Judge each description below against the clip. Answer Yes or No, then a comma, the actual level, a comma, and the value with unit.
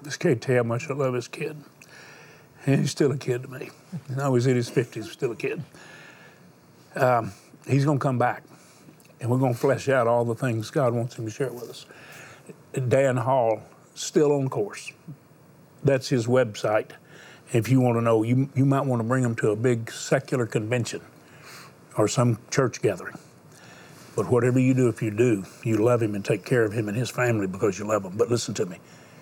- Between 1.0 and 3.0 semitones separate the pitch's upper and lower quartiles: Yes, narrow, 2.6 semitones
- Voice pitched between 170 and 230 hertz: No, low, 130 Hz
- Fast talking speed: Yes, fast, 210 wpm